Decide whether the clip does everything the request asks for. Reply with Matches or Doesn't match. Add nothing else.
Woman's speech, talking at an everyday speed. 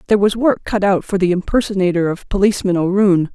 Matches